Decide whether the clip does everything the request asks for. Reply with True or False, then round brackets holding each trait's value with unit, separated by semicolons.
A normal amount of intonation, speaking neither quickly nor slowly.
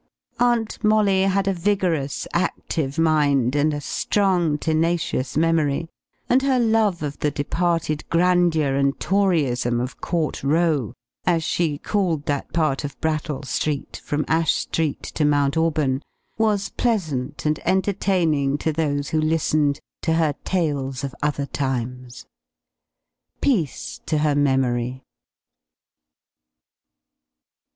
False (3.7 semitones; 120 wpm)